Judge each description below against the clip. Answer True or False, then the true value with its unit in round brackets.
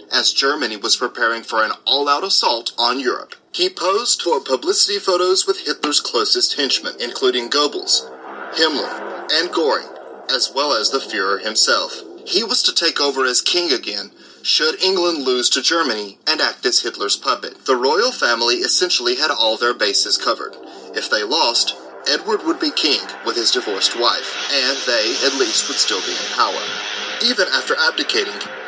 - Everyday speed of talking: True (165 wpm)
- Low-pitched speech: False (360 Hz)